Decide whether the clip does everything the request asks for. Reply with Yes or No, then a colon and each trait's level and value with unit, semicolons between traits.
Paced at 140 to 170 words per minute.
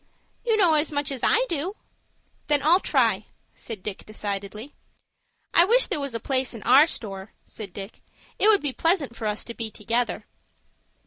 No: average, 180 wpm